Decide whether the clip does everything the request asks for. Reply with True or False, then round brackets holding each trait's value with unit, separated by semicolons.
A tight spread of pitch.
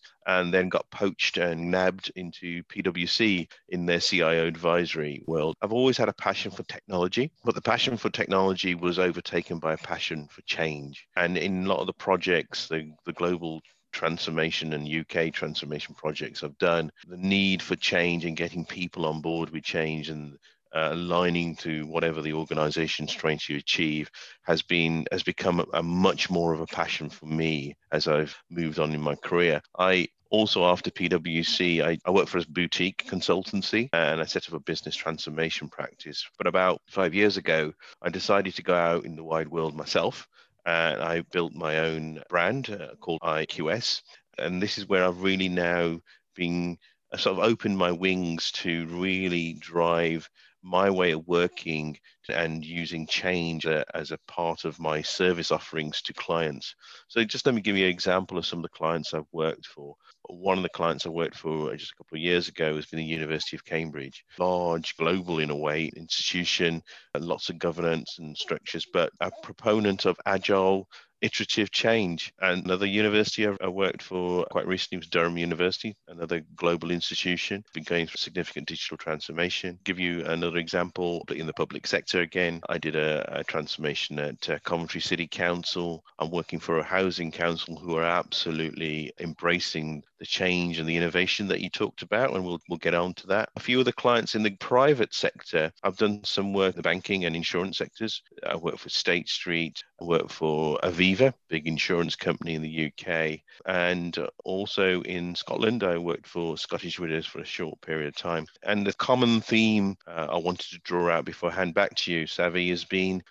True (2.2 semitones)